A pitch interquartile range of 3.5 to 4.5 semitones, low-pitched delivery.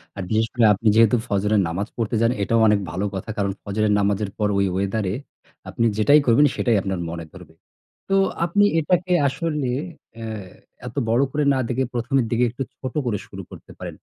Yes: average, 3.8 semitones; low, 110 Hz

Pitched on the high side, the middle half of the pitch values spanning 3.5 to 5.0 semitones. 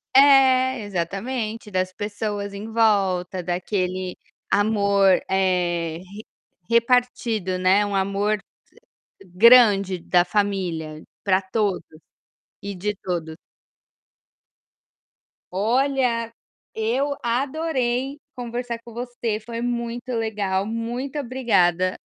Yes: high, 210 Hz; average, 4.2 semitones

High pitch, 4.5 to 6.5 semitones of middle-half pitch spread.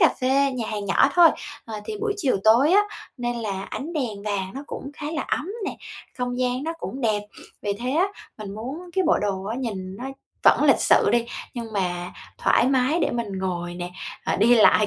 Yes: high, 240 Hz; wide, 5.4 semitones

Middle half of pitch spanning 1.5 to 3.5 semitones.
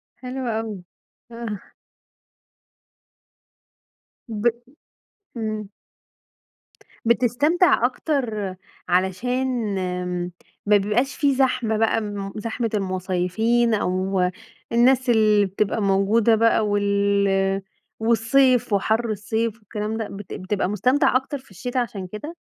Yes: average, 3.1 semitones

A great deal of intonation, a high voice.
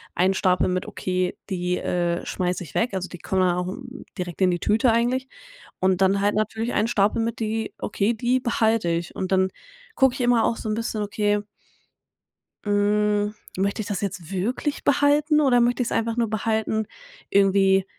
No: average, 3.6 semitones; high, 210 Hz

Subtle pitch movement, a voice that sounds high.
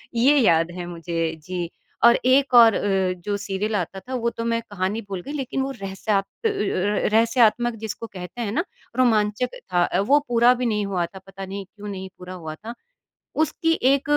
No: average, 4.3 semitones; high, 210 Hz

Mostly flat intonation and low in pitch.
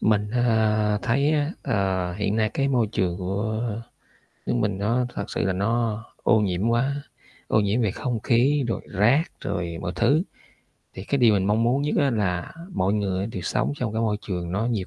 No: average, 3.6 semitones; low, 110 Hz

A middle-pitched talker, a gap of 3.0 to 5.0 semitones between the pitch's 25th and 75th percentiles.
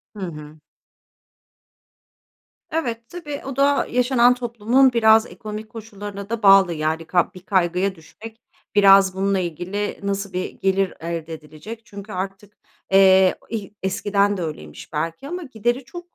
No: high, 200 Hz; average, 3.9 semitones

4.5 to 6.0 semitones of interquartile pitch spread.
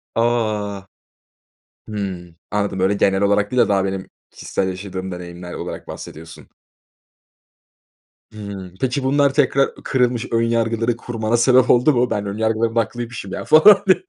No: average, 3.8 semitones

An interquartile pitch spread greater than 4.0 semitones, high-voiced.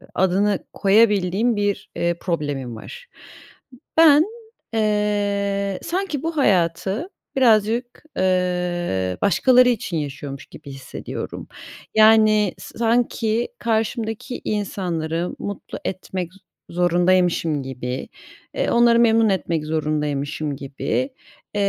Yes: average, 5.1 semitones; high, 195 Hz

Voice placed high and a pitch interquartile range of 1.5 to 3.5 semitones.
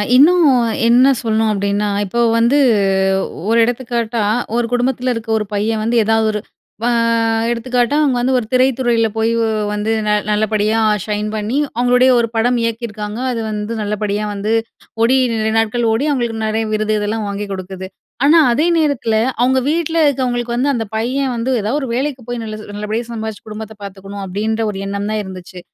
Yes: high, 225 Hz; average, 2.7 semitones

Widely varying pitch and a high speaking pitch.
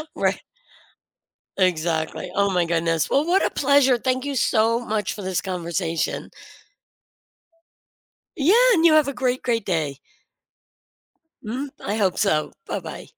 Yes: wide, 7.1 semitones; high, 210 Hz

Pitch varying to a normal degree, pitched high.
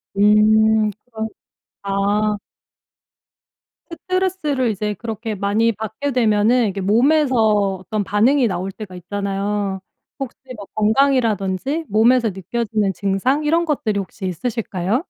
Yes: average, 3.9 semitones; high, 215 Hz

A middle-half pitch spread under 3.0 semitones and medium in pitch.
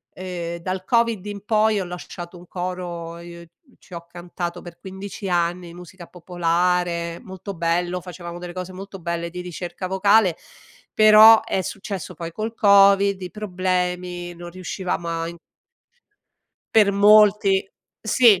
Yes: narrow, 2.4 semitones; medium, 180 Hz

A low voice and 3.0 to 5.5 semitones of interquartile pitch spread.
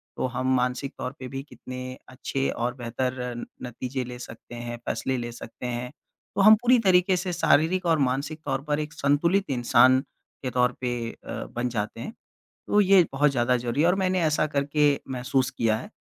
Yes: low, 130 Hz; average, 3.7 semitones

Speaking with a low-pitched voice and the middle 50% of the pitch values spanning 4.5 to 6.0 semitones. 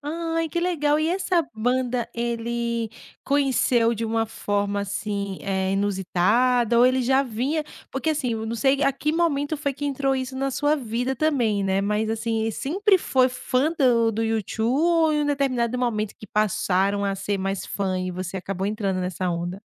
No: high, 235 Hz; average, 5.3 semitones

